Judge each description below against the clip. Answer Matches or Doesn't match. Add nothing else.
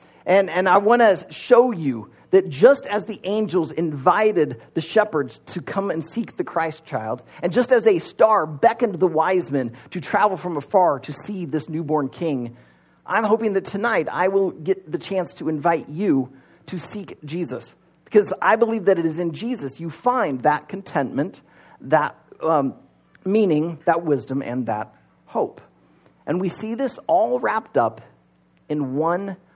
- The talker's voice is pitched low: Doesn't match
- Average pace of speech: Matches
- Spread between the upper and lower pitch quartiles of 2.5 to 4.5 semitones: Doesn't match